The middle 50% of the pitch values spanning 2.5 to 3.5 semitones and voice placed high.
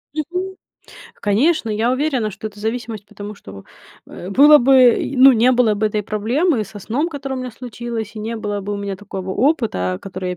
No: average, 4.2 semitones; high, 225 Hz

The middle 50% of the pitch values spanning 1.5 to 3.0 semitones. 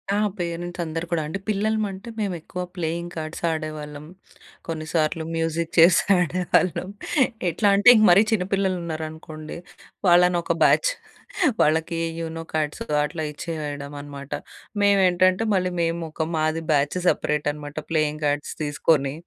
Yes: narrow, 2.6 semitones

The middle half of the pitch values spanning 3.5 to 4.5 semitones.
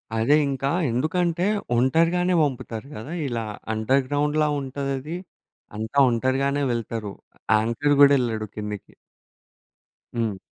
Yes: average, 4.2 semitones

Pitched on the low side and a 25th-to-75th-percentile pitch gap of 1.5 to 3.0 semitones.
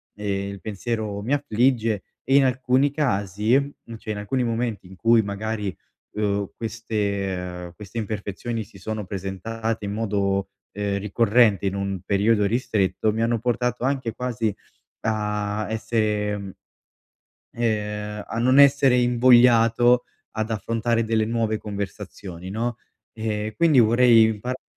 Yes: low, 110 Hz; narrow, 2.6 semitones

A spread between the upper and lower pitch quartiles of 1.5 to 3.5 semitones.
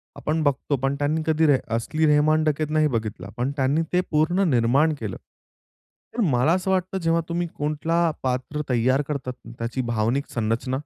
No: average, 4.0 semitones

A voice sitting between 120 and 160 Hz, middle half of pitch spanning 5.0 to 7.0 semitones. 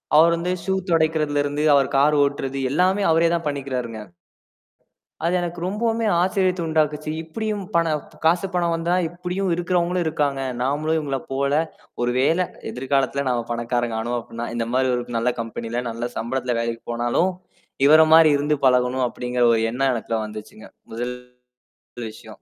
Yes: medium, 140 Hz; wide, 5.5 semitones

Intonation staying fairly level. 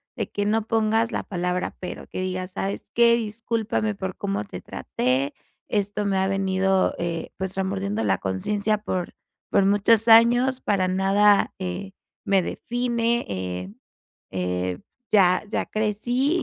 No: average, 3.2 semitones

